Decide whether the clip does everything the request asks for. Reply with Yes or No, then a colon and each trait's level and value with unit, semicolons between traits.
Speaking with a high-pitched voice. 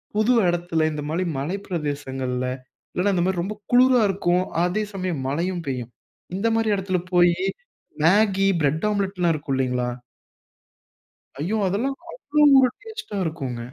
No: medium, 180 Hz